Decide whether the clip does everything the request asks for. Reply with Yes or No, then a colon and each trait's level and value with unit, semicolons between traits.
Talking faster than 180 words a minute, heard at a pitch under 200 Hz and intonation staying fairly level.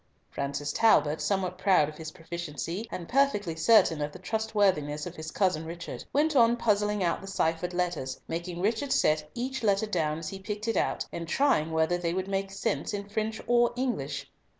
No: average, 190 wpm; medium, 185 Hz; average, 5.0 semitones